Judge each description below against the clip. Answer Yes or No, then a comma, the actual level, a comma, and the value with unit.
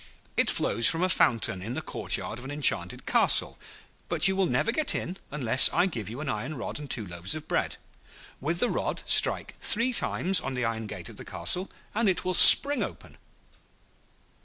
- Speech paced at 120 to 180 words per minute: No, average, 200 wpm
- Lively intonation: Yes, wide, 8.4 semitones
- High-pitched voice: No, medium, 145 Hz